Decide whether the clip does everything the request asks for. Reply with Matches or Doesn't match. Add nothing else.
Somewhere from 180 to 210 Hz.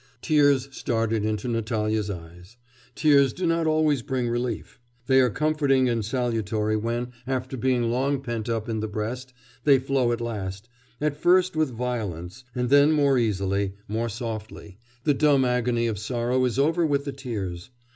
Doesn't match